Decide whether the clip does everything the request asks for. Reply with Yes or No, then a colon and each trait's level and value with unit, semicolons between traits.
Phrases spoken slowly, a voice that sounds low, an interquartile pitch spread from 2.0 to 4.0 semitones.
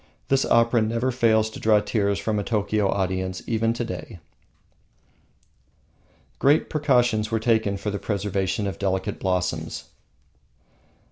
Yes: slow, 130 wpm; low, 105 Hz; average, 3.0 semitones